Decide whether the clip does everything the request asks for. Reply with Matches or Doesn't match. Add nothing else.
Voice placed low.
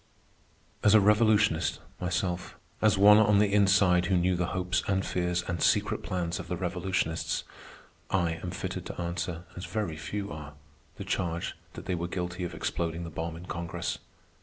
Matches